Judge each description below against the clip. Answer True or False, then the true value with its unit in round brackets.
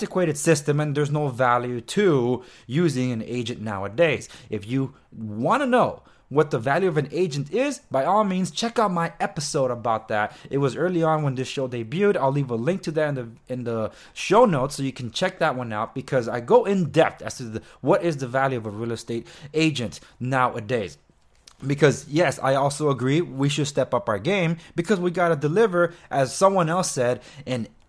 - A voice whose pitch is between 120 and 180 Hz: True (140 Hz)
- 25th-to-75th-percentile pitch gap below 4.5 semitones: False (5.5 semitones)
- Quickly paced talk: True (210 wpm)